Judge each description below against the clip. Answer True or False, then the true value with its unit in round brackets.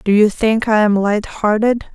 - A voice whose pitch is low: False (215 Hz)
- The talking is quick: False (155 wpm)